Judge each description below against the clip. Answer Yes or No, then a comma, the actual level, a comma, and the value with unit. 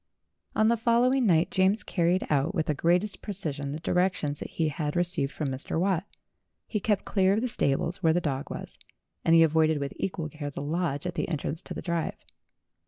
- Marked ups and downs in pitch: No, average, 4.1 semitones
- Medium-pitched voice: Yes, medium, 170 Hz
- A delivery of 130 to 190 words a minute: No, fast, 205 wpm